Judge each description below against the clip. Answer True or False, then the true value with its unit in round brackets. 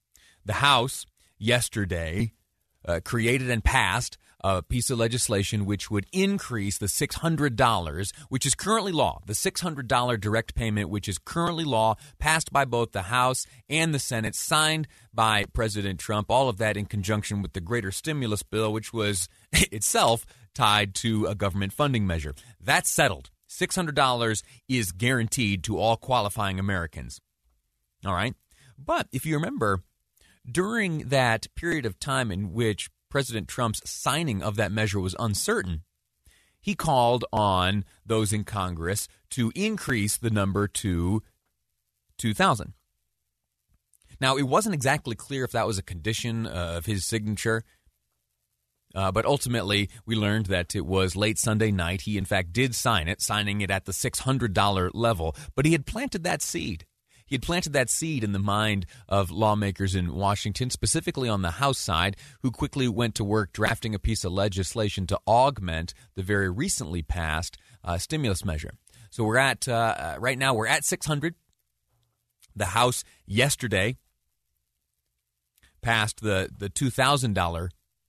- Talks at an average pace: True (150 wpm)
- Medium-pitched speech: False (110 Hz)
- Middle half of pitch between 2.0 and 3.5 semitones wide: False (4.5 semitones)